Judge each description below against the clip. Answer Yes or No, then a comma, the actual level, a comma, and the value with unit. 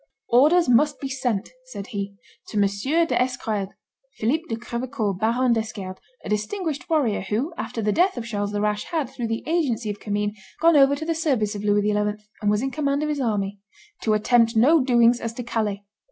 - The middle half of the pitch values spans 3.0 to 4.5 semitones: No, average, 5.0 semitones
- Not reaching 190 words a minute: No, average, 195 wpm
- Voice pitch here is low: No, high, 230 Hz